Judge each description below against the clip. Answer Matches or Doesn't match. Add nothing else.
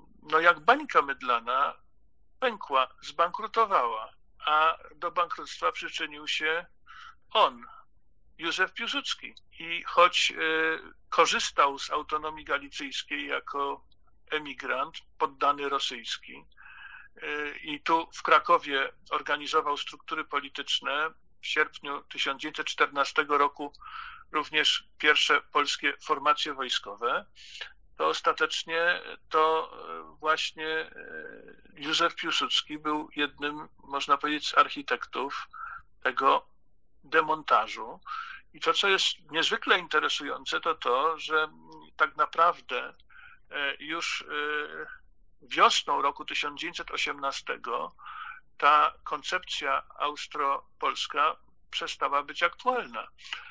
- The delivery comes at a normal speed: Doesn't match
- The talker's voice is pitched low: Doesn't match